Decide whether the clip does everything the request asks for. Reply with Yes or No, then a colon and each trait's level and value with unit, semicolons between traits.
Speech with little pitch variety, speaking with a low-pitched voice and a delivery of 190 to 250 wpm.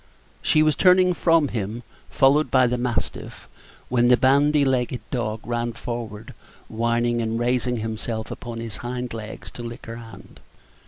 No: narrow, 2.2 semitones; low, 120 Hz; average, 155 wpm